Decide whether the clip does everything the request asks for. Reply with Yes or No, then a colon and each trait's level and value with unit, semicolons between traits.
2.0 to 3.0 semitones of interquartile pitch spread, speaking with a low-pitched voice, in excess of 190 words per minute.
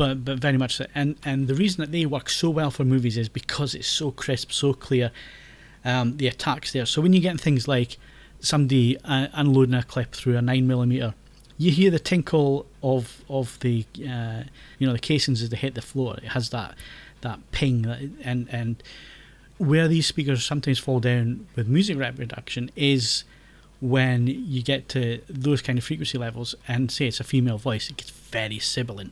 Yes: average, 2.7 semitones; low, 130 Hz; average, 200 wpm